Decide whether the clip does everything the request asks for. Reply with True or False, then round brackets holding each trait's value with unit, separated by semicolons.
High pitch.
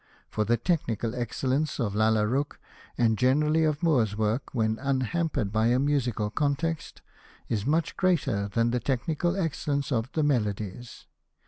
False (125 Hz)